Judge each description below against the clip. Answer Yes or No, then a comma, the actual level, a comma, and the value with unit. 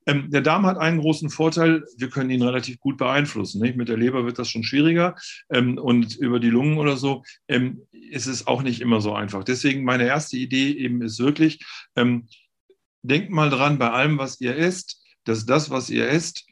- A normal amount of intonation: Yes, average, 3.7 semitones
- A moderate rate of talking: No, fast, 205 wpm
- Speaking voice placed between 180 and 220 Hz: No, low, 130 Hz